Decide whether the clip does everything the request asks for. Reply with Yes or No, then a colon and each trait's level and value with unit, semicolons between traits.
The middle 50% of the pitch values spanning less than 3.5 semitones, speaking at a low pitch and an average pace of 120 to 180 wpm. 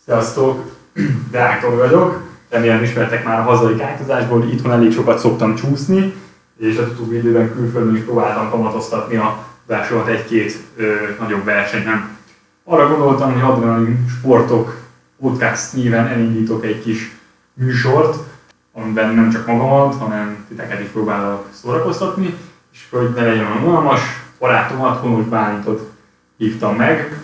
Yes: average, 2.7 semitones; low, 115 Hz; average, 125 wpm